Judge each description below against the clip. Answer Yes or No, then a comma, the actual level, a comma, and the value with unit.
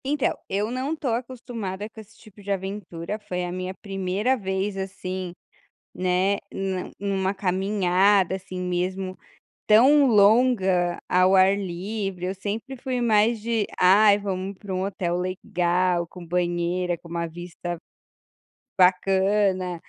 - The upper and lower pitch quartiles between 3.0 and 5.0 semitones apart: No, narrow, 2.4 semitones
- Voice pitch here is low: No, high, 190 Hz